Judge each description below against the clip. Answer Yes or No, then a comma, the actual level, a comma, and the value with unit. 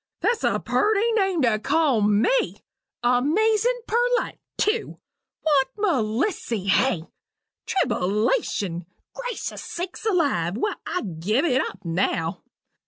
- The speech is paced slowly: Yes, slow, 105 wpm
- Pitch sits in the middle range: No, very high, 290 Hz